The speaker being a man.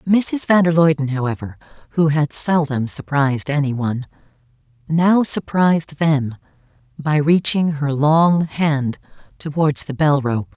No: female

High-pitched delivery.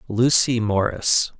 No: low, 115 Hz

